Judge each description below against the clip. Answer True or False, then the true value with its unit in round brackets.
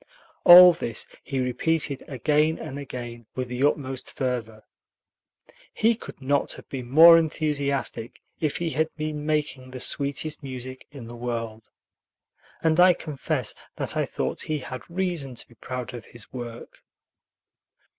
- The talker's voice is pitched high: False (140 Hz)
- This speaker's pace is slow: False (145 wpm)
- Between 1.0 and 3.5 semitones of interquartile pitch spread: False (3.9 semitones)